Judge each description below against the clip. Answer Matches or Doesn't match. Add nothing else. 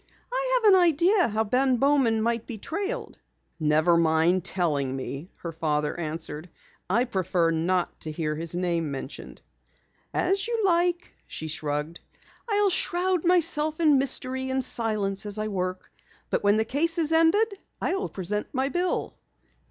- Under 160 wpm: Matches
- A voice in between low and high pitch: Doesn't match